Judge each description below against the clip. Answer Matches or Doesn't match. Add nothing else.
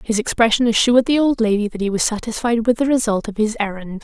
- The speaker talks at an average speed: Doesn't match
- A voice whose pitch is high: Matches